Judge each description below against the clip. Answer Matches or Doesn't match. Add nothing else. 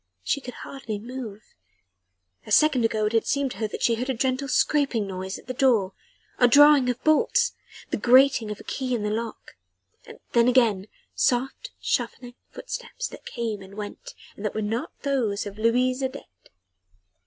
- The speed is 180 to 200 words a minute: Matches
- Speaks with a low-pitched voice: Doesn't match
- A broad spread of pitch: Doesn't match